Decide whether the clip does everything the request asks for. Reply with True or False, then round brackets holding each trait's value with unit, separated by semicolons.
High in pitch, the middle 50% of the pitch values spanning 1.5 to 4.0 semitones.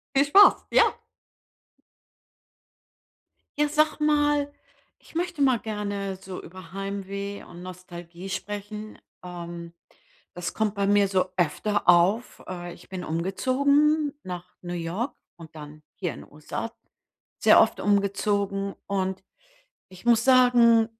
False (200 Hz; 4.7 semitones)